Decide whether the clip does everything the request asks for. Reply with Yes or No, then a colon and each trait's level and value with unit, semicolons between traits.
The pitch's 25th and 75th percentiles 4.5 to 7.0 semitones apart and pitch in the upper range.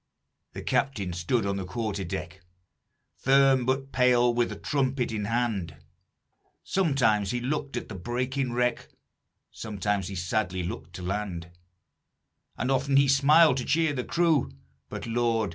No: wide, 5.4 semitones; low, 120 Hz